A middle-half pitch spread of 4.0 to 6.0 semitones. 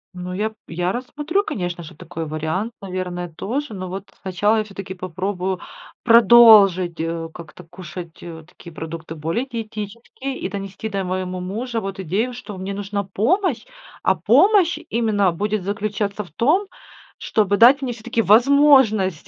Yes: average, 4.3 semitones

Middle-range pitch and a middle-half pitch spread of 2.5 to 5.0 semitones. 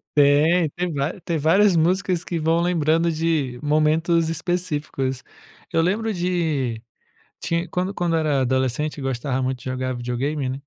Yes: medium, 155 Hz; average, 4.4 semitones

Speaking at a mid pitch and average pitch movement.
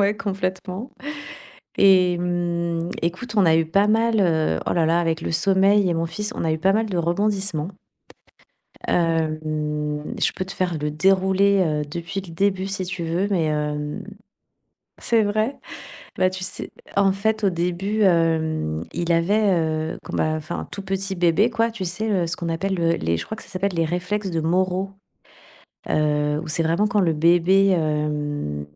Yes: medium, 175 Hz; average, 3.2 semitones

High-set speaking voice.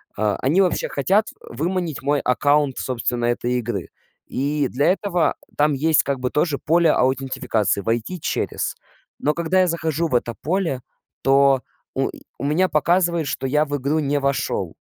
No: medium, 145 Hz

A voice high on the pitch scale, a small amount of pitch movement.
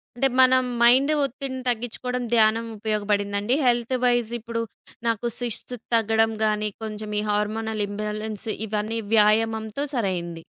Yes: high, 220 Hz; narrow, 2.3 semitones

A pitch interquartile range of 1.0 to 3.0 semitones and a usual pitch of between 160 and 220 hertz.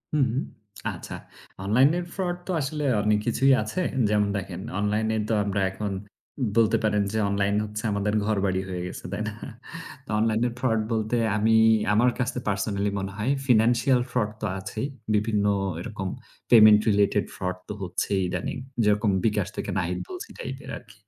No: narrow, 2.6 semitones; low, 105 Hz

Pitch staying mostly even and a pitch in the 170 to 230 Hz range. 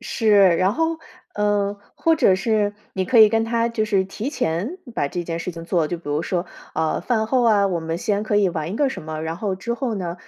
No: average, 4.8 semitones; high, 200 Hz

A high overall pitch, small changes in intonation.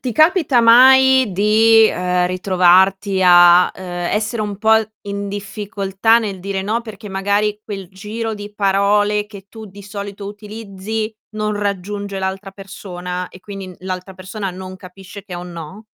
Yes: high, 200 Hz; narrow, 2.1 semitones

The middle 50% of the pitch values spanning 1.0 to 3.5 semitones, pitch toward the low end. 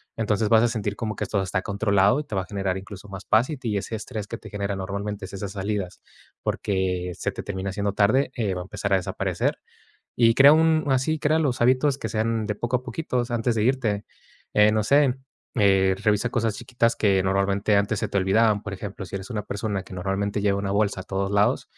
Yes: average, 2.9 semitones; low, 105 Hz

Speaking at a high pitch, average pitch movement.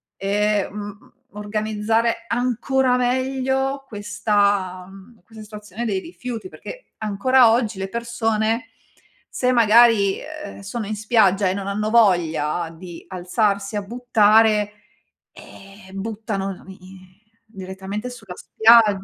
Yes: high, 215 Hz; average, 3.0 semitones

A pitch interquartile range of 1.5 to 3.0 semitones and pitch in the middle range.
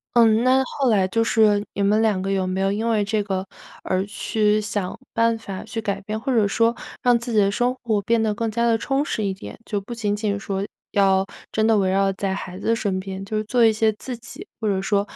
No: narrow, 2.6 semitones; high, 210 Hz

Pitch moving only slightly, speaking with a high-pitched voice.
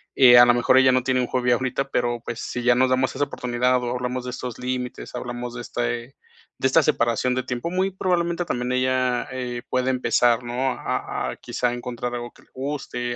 No: narrow, 1.2 semitones; low, 125 Hz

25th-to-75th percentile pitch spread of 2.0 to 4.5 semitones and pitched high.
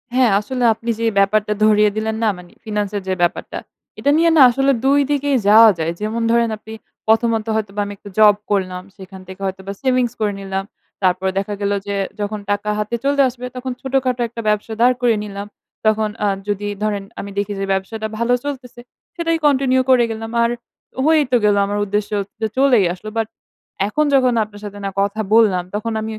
Yes: average, 3.4 semitones; high, 215 Hz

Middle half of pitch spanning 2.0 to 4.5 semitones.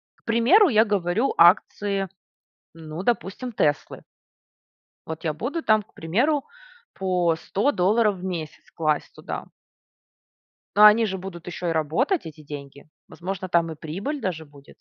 No: average, 5.2 semitones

